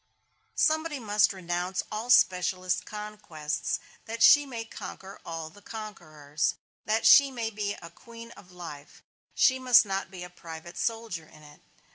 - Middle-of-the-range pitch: No, high, 205 Hz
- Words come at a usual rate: Yes, average, 150 wpm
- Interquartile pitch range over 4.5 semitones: Yes, average, 5.0 semitones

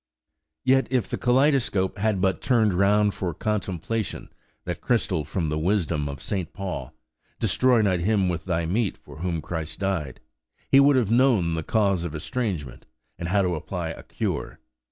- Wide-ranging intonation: No, average, 4.7 semitones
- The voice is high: No, very low, 95 Hz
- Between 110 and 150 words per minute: No, average, 170 wpm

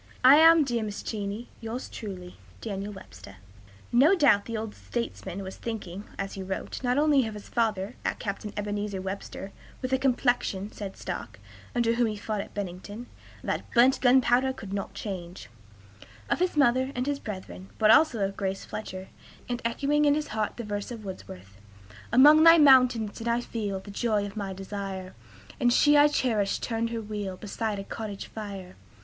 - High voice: Yes, high, 215 Hz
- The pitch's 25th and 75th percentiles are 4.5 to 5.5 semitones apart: No, average, 4.0 semitones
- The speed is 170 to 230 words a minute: Yes, average, 180 wpm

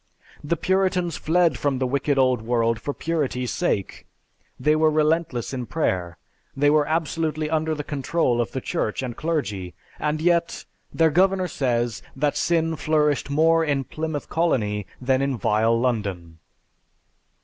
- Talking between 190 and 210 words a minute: No, average, 150 wpm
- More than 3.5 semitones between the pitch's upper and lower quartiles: Yes, average, 4.8 semitones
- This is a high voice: No, medium, 145 Hz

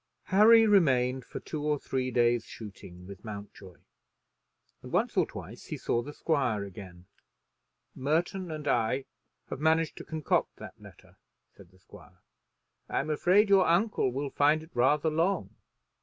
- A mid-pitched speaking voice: Yes, medium, 145 Hz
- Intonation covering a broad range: Yes, wide, 6.0 semitones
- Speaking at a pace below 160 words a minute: Yes, average, 150 wpm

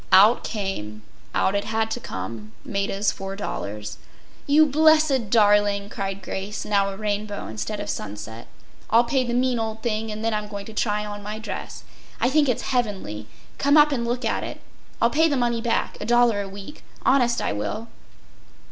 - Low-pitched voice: No, high, 215 Hz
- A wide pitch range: No, average, 3.4 semitones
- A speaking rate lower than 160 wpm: No, average, 175 wpm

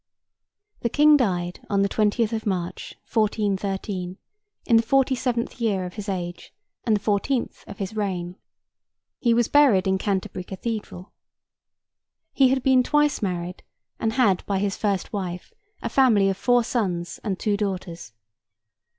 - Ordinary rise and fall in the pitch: Yes, average, 3.9 semitones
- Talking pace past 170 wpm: No, average, 150 wpm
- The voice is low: No, high, 205 Hz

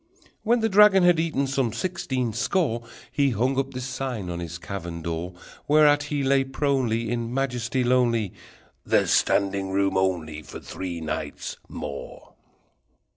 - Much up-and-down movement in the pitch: Yes, wide, 6.4 semitones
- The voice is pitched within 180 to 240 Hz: No, low, 125 Hz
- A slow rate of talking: No, average, 165 wpm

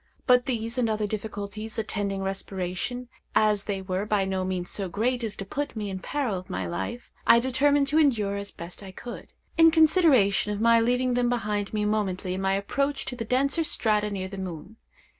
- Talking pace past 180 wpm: Yes, average, 200 wpm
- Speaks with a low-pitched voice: No, high, 210 Hz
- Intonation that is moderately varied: Yes, average, 4.2 semitones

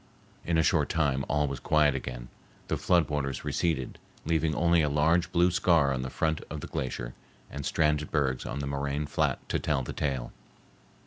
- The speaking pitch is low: Yes, very low, 75 Hz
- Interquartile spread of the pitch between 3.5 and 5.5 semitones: No, average, 2.9 semitones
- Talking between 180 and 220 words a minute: Yes, average, 190 wpm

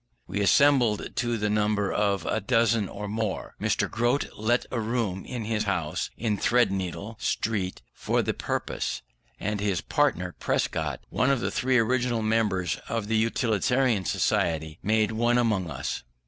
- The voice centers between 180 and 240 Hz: No, low, 110 Hz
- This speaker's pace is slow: No, average, 155 wpm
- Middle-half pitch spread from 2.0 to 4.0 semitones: Yes, average, 3.0 semitones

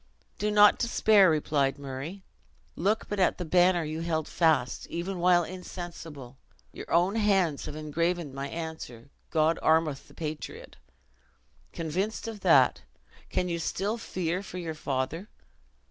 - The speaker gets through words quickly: No, average, 140 wpm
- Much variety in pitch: No, average, 3.4 semitones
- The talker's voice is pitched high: No, medium, 170 Hz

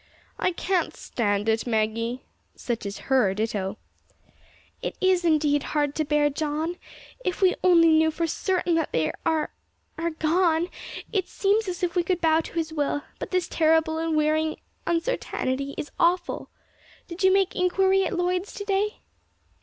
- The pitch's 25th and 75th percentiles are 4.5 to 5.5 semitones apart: No, average, 3.8 semitones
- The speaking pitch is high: Yes, very high, 320 Hz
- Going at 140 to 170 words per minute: Yes, average, 160 wpm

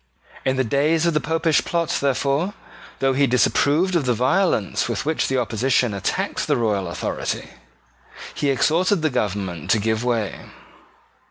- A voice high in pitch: No, low, 135 Hz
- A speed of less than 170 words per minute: Yes, average, 155 wpm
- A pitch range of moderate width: No, wide, 5.7 semitones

